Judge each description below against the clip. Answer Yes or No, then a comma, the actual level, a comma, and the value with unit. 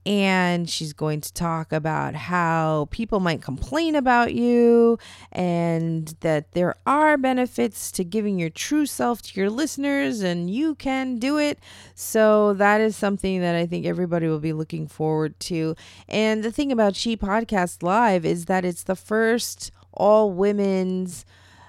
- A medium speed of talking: Yes, average, 160 wpm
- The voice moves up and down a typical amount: No, wide, 5.8 semitones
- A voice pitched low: No, high, 190 Hz